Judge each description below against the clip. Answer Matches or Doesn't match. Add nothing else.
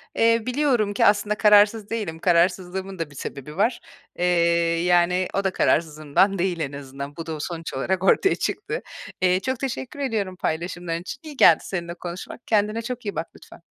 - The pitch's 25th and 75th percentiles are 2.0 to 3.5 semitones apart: Doesn't match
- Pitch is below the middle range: Doesn't match